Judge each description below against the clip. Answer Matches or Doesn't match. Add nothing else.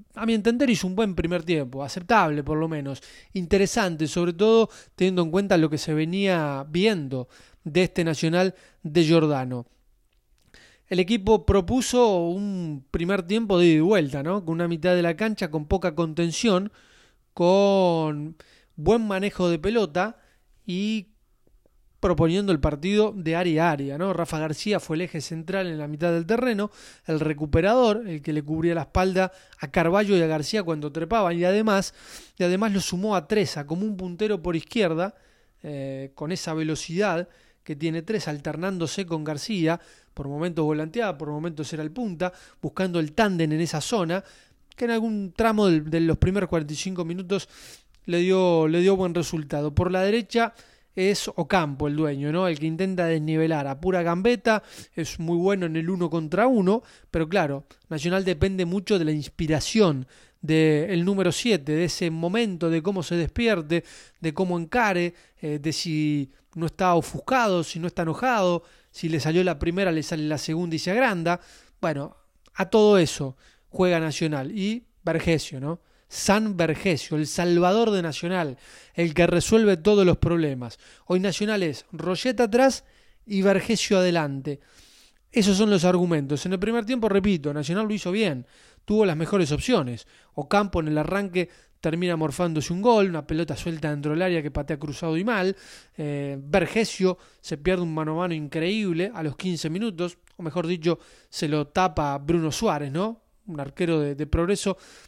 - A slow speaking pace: Doesn't match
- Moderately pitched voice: Matches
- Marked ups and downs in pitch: Doesn't match